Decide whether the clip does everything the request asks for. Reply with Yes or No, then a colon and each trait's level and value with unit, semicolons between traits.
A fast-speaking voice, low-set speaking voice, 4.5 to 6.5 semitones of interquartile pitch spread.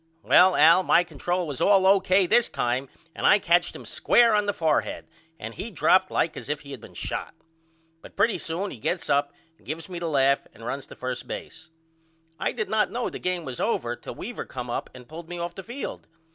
No: fast, 225 wpm; medium, 170 Hz; wide, 5.5 semitones